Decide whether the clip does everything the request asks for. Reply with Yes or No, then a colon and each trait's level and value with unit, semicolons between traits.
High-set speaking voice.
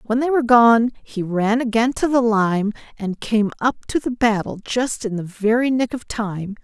Yes: high, 225 Hz